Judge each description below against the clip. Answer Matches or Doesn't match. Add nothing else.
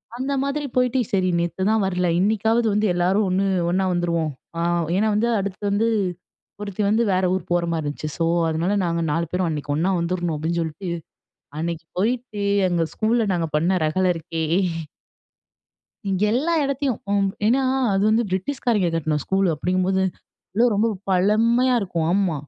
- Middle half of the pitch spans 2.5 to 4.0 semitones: Doesn't match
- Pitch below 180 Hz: Doesn't match